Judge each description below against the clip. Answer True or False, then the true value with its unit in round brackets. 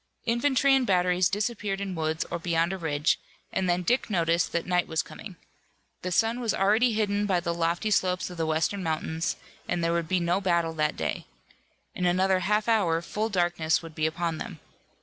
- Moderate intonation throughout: True (3.4 semitones)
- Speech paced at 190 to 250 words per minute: True (195 wpm)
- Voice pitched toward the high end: False (180 Hz)